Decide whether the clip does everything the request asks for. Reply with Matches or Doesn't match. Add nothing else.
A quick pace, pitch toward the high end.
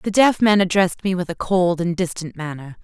Doesn't match